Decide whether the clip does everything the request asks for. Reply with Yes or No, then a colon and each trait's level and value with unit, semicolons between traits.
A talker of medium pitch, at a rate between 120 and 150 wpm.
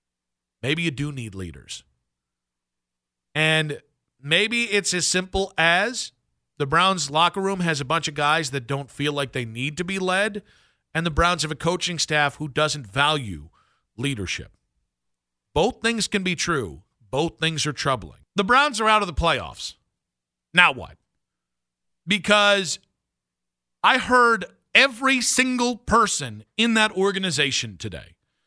Yes: medium, 150 Hz; average, 145 wpm